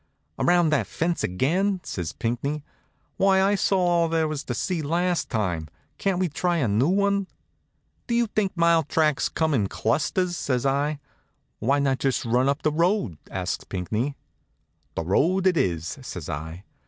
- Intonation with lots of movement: Yes, wide, 7.3 semitones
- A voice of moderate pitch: Yes, medium, 150 Hz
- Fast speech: No, average, 165 wpm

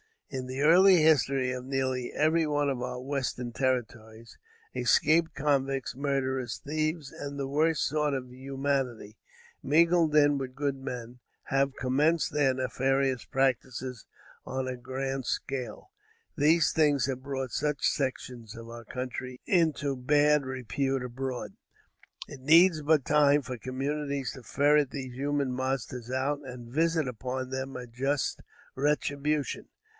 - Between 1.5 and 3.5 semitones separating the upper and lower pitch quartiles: Yes, narrow, 2.4 semitones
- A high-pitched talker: No, low, 135 Hz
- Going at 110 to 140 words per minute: Yes, slow, 135 wpm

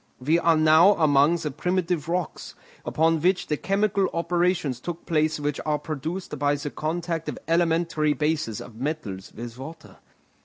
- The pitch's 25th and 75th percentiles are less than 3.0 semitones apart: Yes, narrow, 2.6 semitones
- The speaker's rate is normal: Yes, average, 155 wpm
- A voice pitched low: No, medium, 160 Hz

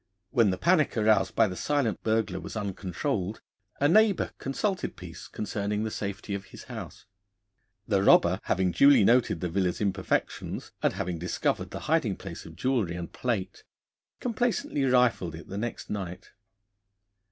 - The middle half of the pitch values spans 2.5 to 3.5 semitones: No, wide, 5.4 semitones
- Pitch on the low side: Yes, low, 105 Hz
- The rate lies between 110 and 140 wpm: No, average, 150 wpm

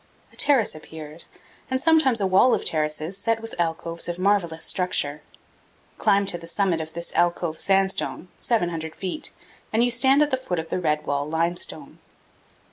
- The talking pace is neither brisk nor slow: Yes, average, 170 wpm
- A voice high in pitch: No, medium, 180 Hz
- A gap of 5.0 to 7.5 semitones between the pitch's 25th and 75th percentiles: Yes, average, 5.3 semitones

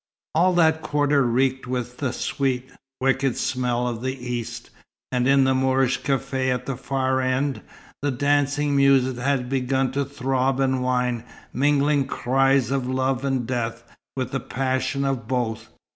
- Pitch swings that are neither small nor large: No, narrow, 1.5 semitones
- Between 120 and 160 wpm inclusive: Yes, average, 155 wpm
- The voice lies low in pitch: Yes, low, 130 Hz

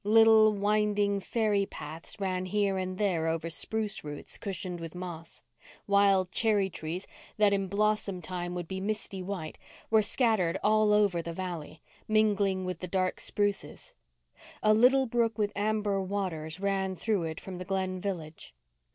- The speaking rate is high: No, average, 155 wpm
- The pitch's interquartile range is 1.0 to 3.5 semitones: Yes, average, 2.7 semitones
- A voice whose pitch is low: No, high, 195 Hz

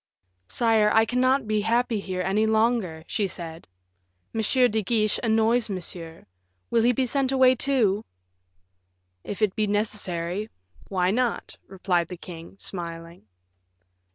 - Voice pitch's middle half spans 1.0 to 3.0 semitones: No, average, 4.2 semitones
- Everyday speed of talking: No, slow, 130 wpm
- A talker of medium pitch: No, high, 215 Hz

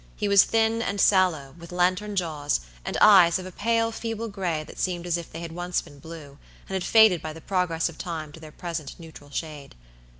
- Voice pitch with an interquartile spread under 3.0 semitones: No, average, 3.6 semitones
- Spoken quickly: Yes, fast, 220 wpm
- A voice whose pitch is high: No, medium, 175 Hz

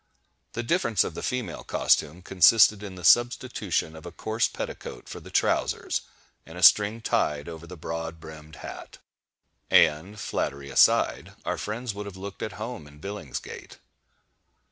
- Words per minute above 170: No, average, 150 wpm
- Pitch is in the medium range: No, very low, 95 Hz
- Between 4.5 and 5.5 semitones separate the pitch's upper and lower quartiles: Yes, average, 5.2 semitones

